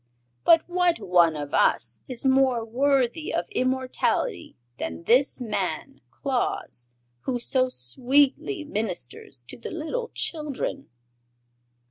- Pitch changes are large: Yes, wide, 8.4 semitones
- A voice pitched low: No, very high, 255 Hz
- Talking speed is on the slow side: Yes, slow, 110 wpm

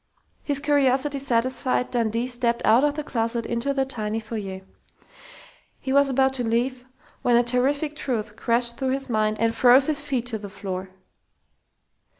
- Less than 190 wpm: Yes, average, 160 wpm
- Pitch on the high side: Yes, high, 245 Hz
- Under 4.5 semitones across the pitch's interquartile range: Yes, average, 2.9 semitones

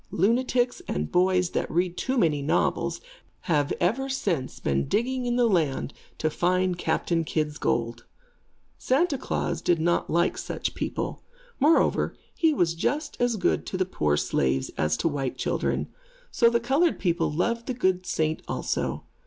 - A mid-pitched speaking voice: Yes, medium, 180 Hz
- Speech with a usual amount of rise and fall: No, wide, 7.7 semitones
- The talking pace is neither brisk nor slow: Yes, average, 160 wpm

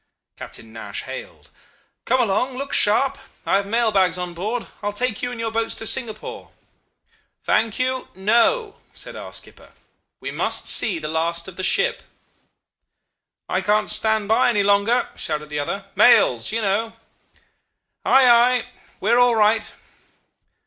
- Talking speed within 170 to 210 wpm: No, average, 155 wpm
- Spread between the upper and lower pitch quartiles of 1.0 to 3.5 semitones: No, average, 4.0 semitones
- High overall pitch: Yes, high, 220 Hz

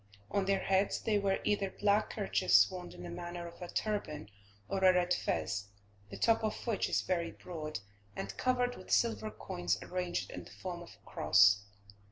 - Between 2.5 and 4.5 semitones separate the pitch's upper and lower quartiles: Yes, average, 3.3 semitones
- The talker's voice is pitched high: No, medium, 180 Hz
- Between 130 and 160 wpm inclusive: No, average, 190 wpm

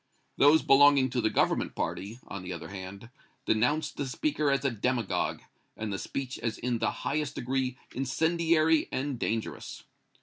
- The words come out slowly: No, average, 160 wpm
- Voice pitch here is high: No, low, 130 Hz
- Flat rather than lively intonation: No, average, 4.6 semitones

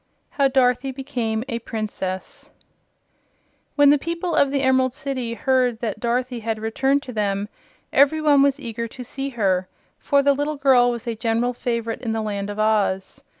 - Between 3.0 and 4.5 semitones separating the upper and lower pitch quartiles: Yes, average, 3.7 semitones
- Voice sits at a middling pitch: No, high, 245 Hz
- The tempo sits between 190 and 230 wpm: No, average, 175 wpm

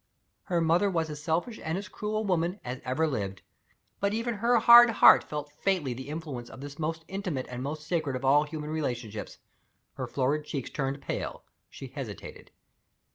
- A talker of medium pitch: Yes, medium, 155 Hz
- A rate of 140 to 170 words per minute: No, average, 185 wpm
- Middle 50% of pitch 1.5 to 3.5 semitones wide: No, wide, 5.5 semitones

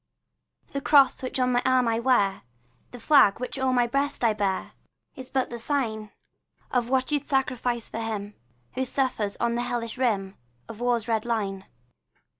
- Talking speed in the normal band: Yes, average, 180 wpm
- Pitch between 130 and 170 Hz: No, high, 240 Hz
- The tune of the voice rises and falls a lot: No, average, 2.8 semitones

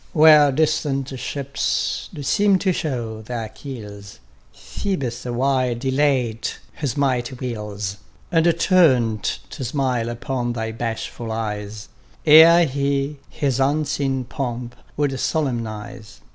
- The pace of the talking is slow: Yes, slow, 110 wpm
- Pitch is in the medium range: No, low, 130 Hz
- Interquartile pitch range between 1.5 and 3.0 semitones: No, average, 4.0 semitones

